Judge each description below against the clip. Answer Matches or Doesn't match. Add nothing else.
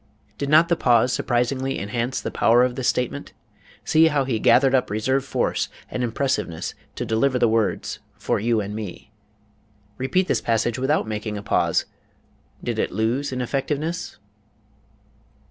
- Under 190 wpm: Matches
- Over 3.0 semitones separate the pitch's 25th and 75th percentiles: Matches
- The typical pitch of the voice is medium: Doesn't match